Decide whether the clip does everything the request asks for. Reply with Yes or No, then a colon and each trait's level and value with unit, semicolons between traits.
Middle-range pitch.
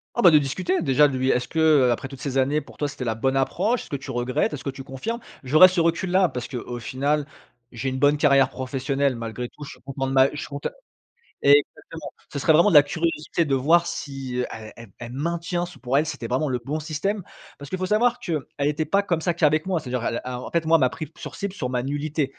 Yes: medium, 145 Hz